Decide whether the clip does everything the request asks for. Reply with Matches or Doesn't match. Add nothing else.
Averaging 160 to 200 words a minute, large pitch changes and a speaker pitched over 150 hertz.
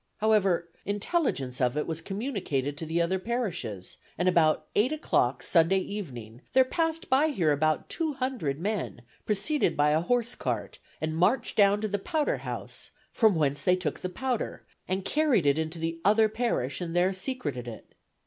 Matches